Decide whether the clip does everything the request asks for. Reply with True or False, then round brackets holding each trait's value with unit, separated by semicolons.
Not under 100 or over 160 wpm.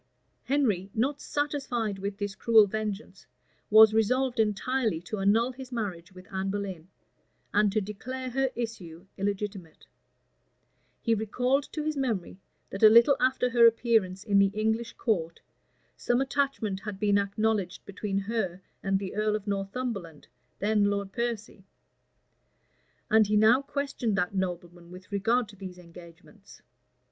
True (140 wpm)